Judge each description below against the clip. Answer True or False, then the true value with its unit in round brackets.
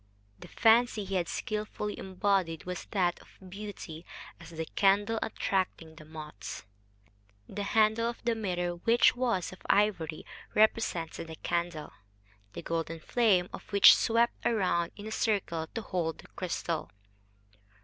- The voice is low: False (190 Hz)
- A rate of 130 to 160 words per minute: True (140 wpm)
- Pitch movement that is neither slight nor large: True (4.3 semitones)